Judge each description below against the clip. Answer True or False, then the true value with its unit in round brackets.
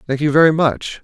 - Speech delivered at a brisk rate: True (230 wpm)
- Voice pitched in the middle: True (145 Hz)